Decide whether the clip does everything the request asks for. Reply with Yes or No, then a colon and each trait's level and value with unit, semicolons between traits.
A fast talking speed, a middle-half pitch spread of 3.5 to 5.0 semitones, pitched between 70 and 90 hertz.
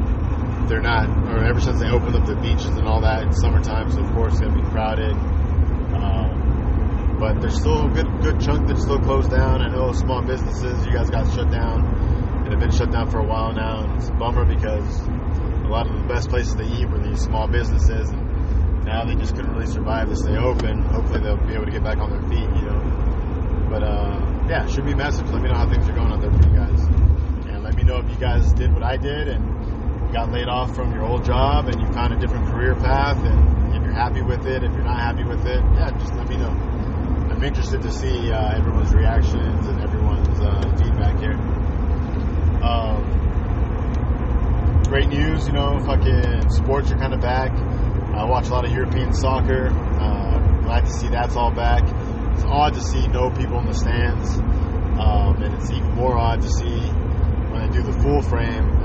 No: fast, 215 wpm; average, 2.9 semitones; very low, 80 Hz